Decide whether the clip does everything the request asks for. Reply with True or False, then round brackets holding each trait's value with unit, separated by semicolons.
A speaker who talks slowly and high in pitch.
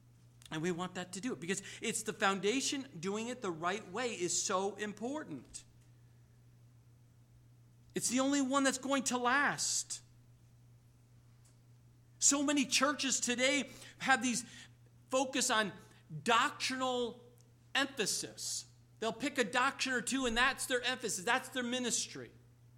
True (130 wpm; 195 Hz)